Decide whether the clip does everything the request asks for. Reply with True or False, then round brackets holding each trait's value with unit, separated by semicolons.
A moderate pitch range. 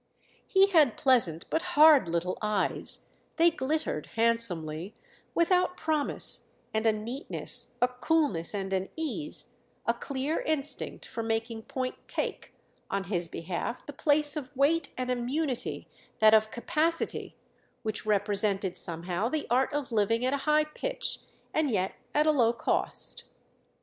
False (6.6 semitones)